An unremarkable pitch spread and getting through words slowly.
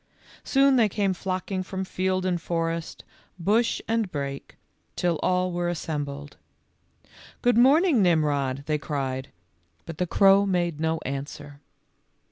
Yes: average, 4.7 semitones; slow, 130 wpm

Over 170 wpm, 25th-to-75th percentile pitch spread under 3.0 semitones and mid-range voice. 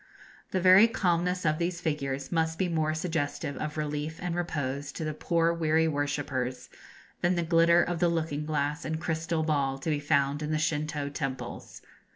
Yes: average, 180 wpm; narrow, 2.5 semitones; medium, 155 Hz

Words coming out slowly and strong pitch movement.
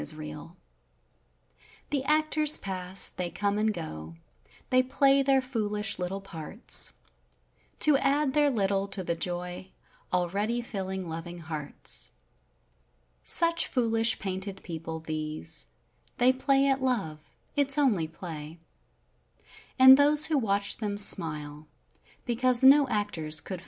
Yes: slow, 110 wpm; wide, 7.6 semitones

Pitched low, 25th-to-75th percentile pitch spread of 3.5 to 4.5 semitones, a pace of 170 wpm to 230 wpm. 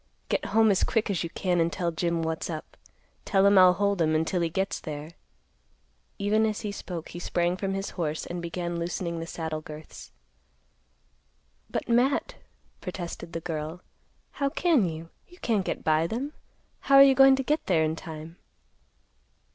No: medium, 175 Hz; average, 3.9 semitones; average, 175 wpm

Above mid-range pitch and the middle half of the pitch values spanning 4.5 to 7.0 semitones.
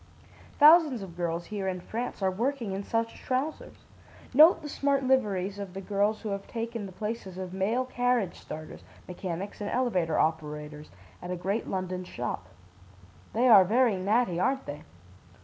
Yes: high, 200 Hz; average, 5.1 semitones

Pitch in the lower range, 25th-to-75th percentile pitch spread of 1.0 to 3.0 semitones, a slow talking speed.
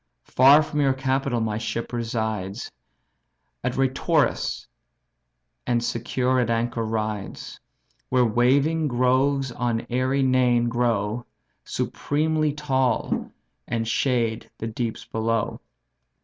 Yes: low, 125 Hz; average, 2.7 semitones; slow, 105 wpm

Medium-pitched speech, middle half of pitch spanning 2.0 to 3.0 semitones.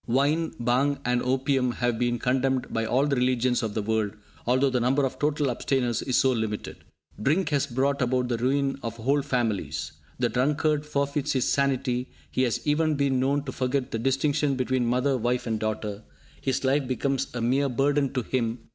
No: low, 130 Hz; narrow, 2.4 semitones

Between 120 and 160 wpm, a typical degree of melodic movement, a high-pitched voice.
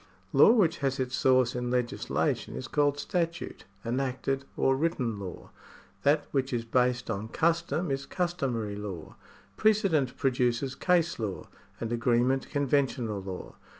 No: slow, 135 wpm; average, 3.8 semitones; low, 130 Hz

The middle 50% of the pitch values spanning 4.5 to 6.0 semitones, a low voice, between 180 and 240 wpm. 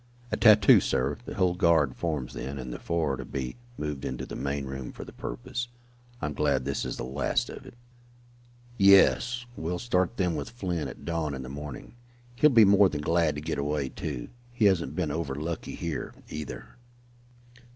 Yes: average, 5.0 semitones; very low, 80 Hz; average, 195 wpm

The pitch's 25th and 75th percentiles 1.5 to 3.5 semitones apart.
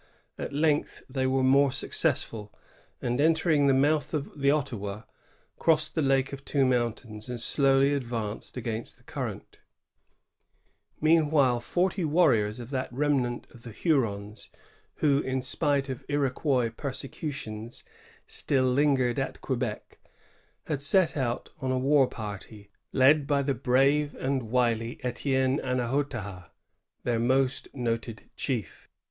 Yes: average, 3.2 semitones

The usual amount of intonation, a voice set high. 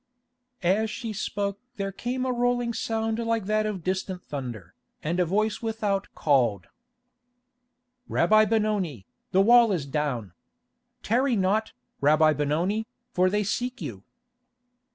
No: wide, 5.9 semitones; high, 200 Hz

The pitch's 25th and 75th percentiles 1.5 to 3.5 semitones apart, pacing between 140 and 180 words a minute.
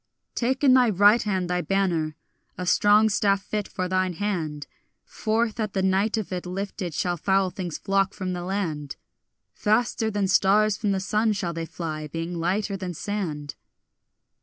Yes: average, 2.9 semitones; average, 170 wpm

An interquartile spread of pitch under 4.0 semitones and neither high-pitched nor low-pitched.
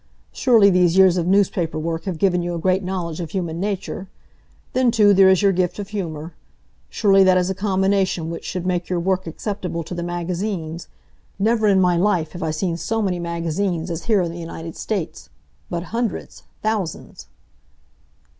Yes: average, 2.7 semitones; medium, 180 Hz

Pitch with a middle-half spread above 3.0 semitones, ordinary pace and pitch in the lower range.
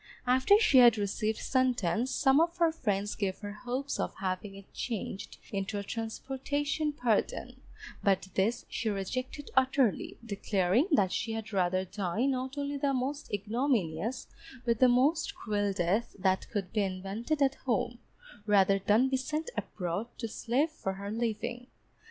No: average, 4.9 semitones; average, 155 wpm; high, 230 Hz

